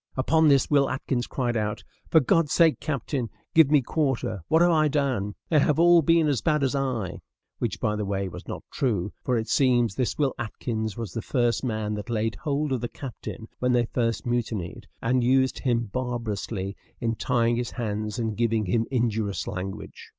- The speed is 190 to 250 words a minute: Yes, average, 195 wpm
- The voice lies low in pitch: Yes, low, 120 Hz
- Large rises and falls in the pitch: No, average, 3.9 semitones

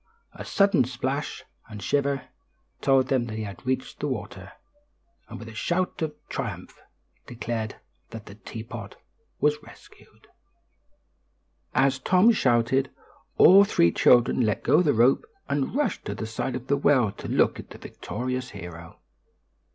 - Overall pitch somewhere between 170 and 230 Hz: No, low, 130 Hz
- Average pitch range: Yes, average, 4.1 semitones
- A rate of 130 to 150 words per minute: Yes, average, 145 wpm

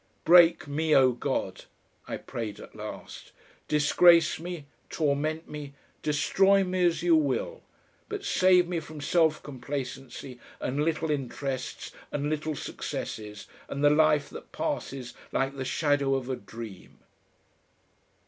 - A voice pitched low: No, medium, 150 Hz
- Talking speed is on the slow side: Yes, slow, 130 wpm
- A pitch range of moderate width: Yes, average, 3.3 semitones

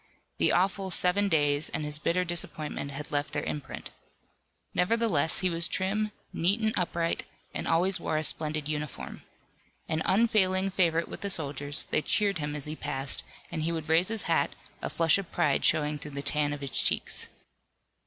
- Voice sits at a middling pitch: Yes, medium, 165 Hz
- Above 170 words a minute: Yes, average, 180 wpm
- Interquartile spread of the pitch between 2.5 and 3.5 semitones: No, average, 4.0 semitones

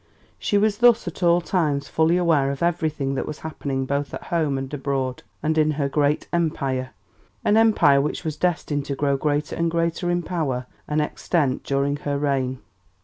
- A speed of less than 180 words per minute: No, average, 185 wpm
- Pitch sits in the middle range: Yes, medium, 150 Hz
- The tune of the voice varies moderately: Yes, average, 3.4 semitones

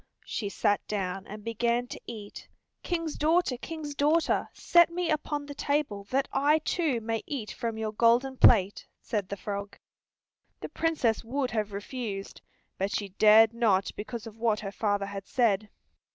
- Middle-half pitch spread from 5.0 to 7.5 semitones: Yes, wide, 5.6 semitones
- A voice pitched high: Yes, high, 230 Hz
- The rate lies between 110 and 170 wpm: Yes, average, 165 wpm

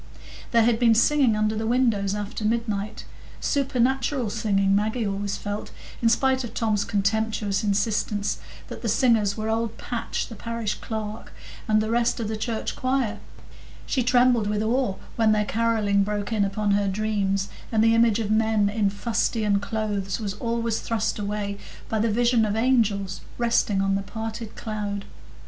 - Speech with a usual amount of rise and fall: No, narrow, 2.2 semitones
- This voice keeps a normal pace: Yes, average, 165 wpm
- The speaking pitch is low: No, high, 220 Hz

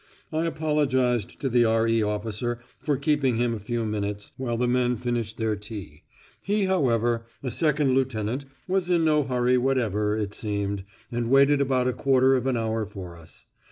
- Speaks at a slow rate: No, average, 175 wpm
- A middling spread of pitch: Yes, average, 3.7 semitones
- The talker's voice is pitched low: Yes, low, 120 Hz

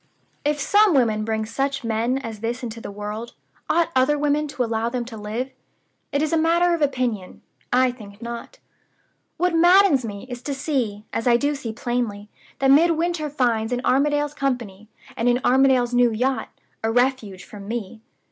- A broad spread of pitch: No, average, 4.4 semitones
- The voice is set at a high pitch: Yes, very high, 250 Hz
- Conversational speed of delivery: Yes, average, 175 wpm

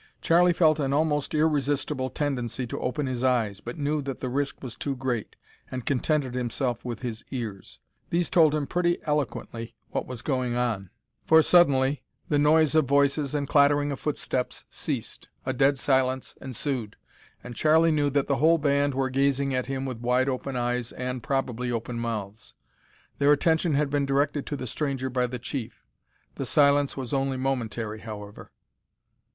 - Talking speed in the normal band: Yes, average, 170 wpm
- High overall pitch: No, low, 135 Hz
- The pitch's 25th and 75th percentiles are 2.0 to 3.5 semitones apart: Yes, average, 2.8 semitones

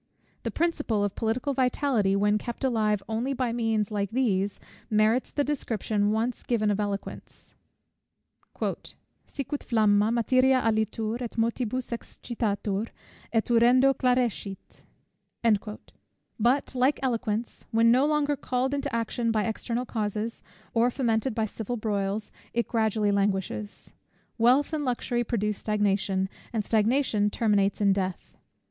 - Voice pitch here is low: No, high, 225 Hz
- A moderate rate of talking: No, slow, 125 wpm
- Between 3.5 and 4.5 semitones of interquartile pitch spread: No, average, 3.1 semitones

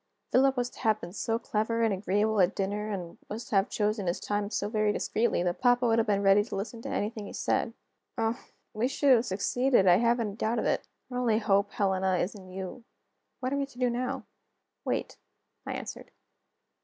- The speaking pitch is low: No, high, 215 Hz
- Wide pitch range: No, average, 3.1 semitones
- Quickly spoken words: Yes, fast, 215 wpm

